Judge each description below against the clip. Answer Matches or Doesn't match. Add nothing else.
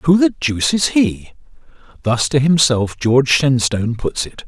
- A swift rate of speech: Doesn't match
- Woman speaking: Doesn't match